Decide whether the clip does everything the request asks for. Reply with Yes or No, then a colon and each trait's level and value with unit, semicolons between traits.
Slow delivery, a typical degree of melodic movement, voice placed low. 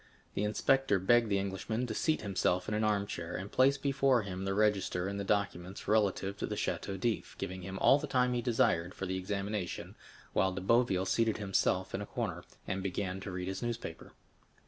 No: average, 195 wpm; average, 3.4 semitones; low, 100 Hz